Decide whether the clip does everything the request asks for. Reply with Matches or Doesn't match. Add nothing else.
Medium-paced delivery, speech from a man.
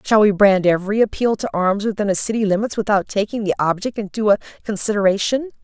Doesn't match